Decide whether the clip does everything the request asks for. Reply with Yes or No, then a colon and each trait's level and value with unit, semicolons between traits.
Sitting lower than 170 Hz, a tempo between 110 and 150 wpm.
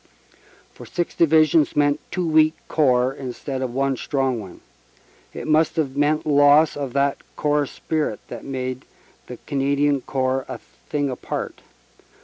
Yes: medium, 140 Hz; average, 140 wpm